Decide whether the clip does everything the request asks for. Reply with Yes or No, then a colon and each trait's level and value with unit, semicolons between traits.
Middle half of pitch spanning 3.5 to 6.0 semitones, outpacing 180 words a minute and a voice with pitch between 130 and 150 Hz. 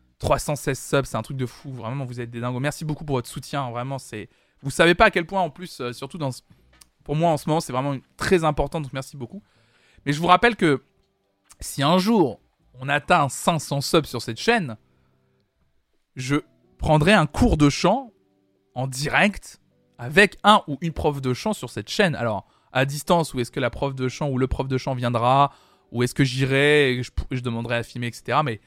Yes: average, 4.3 semitones; fast, 220 wpm; medium, 140 Hz